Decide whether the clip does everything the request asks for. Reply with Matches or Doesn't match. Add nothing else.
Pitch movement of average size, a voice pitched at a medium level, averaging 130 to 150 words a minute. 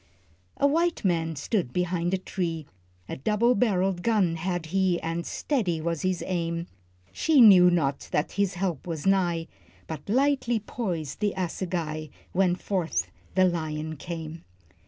Matches